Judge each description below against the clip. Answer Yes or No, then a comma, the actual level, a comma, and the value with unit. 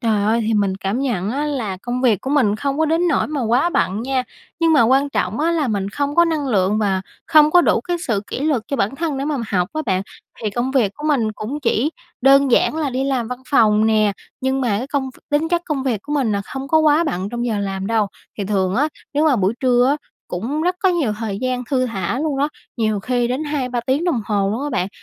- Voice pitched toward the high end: Yes, very high, 255 Hz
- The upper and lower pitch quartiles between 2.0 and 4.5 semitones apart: No, wide, 5.4 semitones